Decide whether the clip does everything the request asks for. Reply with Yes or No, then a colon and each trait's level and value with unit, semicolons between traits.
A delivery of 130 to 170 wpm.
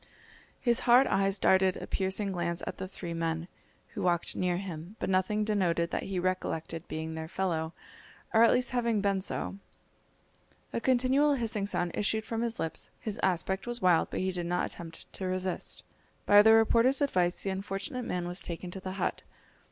No: average, 185 wpm